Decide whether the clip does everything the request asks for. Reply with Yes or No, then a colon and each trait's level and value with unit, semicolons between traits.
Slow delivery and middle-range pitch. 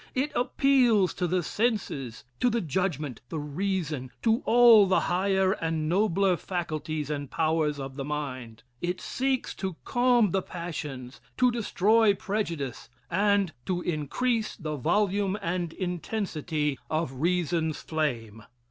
Yes: slow, 130 wpm; medium, 175 Hz